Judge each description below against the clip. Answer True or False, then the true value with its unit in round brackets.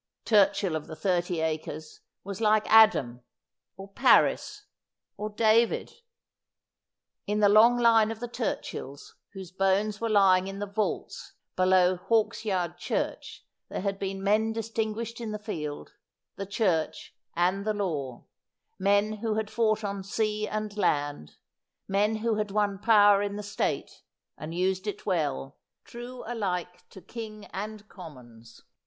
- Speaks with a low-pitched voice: False (200 Hz)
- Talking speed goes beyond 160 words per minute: False (140 wpm)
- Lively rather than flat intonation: False (3.0 semitones)